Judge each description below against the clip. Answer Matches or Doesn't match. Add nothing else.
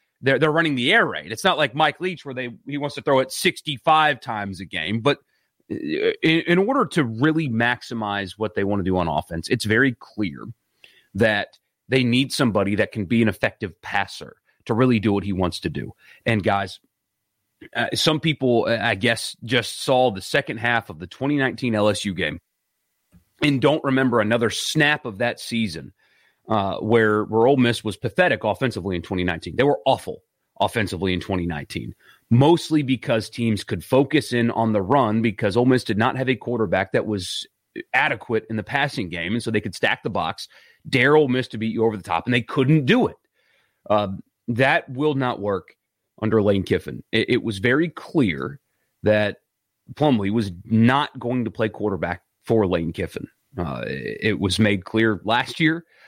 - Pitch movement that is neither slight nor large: Matches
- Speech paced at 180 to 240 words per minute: Matches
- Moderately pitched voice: Doesn't match